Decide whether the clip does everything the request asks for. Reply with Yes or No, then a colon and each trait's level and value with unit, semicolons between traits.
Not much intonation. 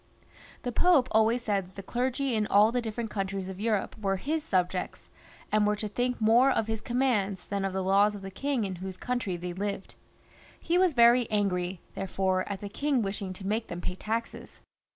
No: average, 3.8 semitones